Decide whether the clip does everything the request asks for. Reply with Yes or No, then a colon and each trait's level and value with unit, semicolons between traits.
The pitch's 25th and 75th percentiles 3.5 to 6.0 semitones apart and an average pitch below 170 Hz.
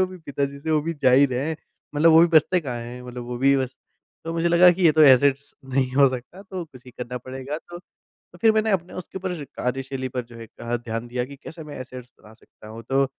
Yes: average, 4.7 semitones; medium, 140 Hz